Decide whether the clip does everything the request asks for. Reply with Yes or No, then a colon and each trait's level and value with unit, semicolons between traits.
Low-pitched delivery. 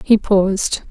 No: high, 200 Hz